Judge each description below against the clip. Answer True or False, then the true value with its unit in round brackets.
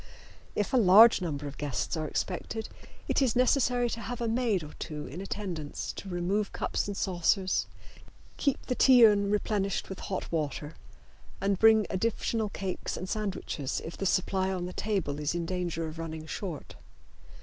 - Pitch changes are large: False (4.7 semitones)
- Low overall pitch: False (190 Hz)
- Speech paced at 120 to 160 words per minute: False (175 wpm)